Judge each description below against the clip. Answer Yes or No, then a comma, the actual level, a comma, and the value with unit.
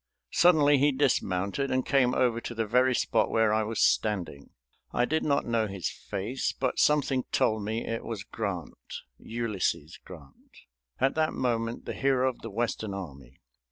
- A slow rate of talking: No, average, 165 wpm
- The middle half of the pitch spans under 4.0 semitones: No, average, 4.4 semitones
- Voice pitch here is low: Yes, low, 115 Hz